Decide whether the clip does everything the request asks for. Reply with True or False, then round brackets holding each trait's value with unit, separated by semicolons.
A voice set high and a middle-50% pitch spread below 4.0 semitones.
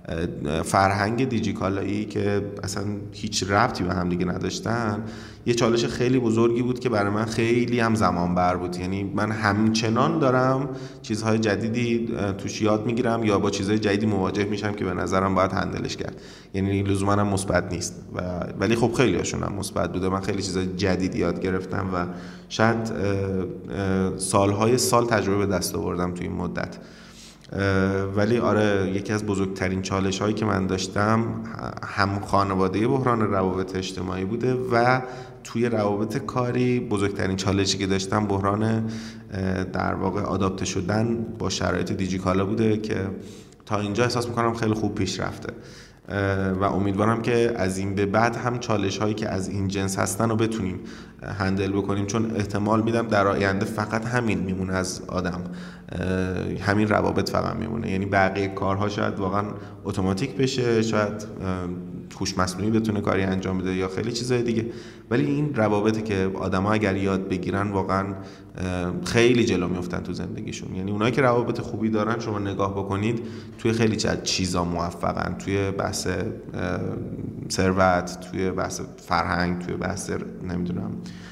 False (100 Hz; 2.9 semitones)